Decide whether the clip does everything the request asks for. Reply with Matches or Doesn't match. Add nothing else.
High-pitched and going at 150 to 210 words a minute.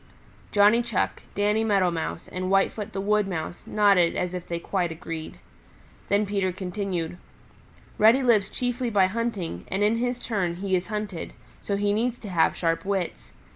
Matches